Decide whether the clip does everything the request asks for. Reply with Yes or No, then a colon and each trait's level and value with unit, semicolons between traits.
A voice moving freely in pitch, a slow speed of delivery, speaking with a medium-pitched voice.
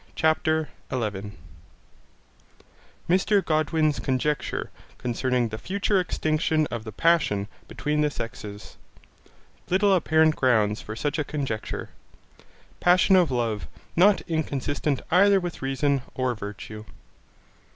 Yes: wide, 6.0 semitones; slow, 110 wpm; medium, 145 Hz